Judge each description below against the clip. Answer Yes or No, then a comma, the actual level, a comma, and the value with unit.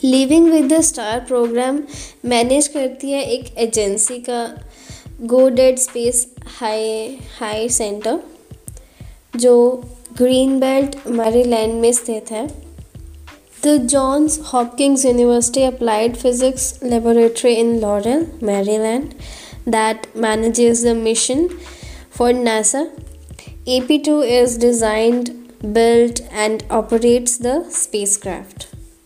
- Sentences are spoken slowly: Yes, slow, 105 wpm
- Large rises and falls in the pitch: No, average, 2.7 semitones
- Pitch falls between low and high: No, high, 240 Hz